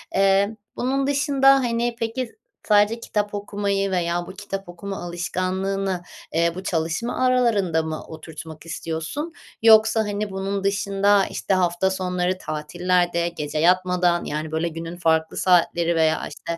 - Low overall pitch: No, medium, 185 Hz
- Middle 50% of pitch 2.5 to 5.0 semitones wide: Yes, average, 3.3 semitones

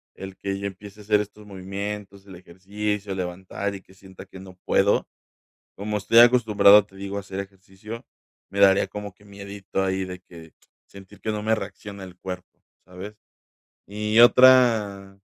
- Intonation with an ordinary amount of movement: No, narrow, 1.5 semitones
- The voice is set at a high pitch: No, low, 100 Hz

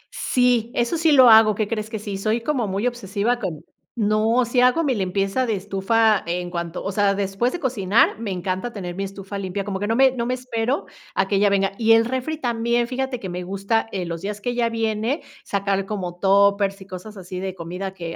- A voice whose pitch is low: No, high, 210 Hz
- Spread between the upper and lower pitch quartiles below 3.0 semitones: No, average, 3.6 semitones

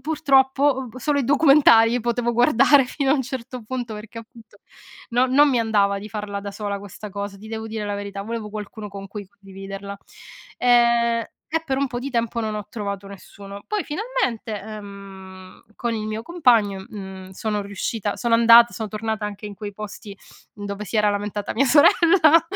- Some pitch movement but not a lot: Yes, average, 3.5 semitones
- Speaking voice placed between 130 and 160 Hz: No, high, 220 Hz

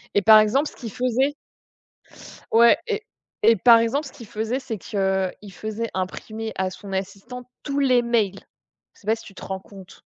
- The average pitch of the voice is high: Yes, high, 220 Hz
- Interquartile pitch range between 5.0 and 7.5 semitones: No, average, 3.8 semitones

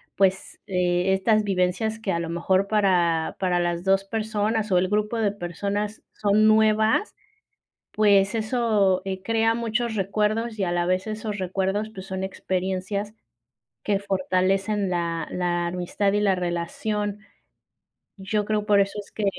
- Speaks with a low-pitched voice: No, high, 195 Hz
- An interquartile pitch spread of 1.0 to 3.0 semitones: Yes, narrow, 2.6 semitones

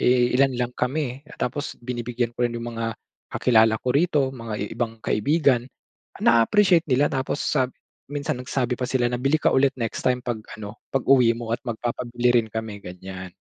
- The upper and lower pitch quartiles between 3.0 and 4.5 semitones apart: No, narrow, 2.5 semitones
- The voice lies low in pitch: Yes, low, 125 Hz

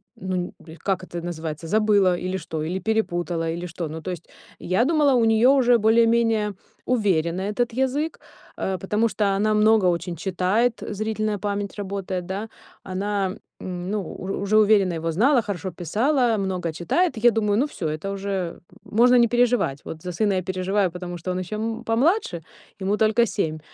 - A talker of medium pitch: No, high, 200 Hz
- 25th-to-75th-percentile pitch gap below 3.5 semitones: No, average, 3.8 semitones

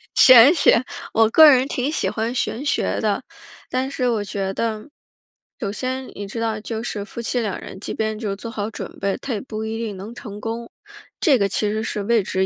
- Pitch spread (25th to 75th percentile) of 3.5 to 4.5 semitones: No, average, 3.1 semitones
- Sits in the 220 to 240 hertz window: Yes, high, 225 Hz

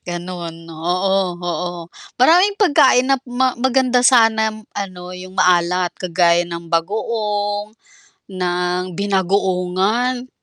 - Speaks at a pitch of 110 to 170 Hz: No, high, 190 Hz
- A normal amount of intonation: Yes, average, 5.0 semitones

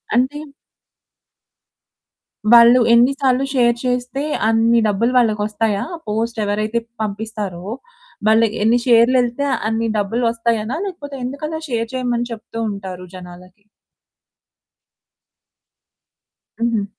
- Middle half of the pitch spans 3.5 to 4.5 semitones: No, narrow, 2.6 semitones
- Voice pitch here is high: Yes, high, 230 Hz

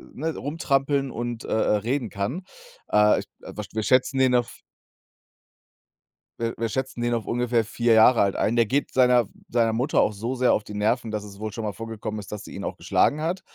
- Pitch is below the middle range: Yes, low, 115 Hz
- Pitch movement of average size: Yes, average, 3.2 semitones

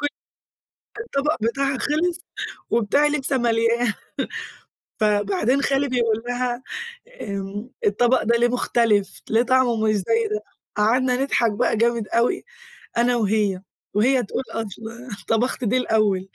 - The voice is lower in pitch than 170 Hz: No, high, 235 Hz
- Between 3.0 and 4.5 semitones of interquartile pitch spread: Yes, average, 3.3 semitones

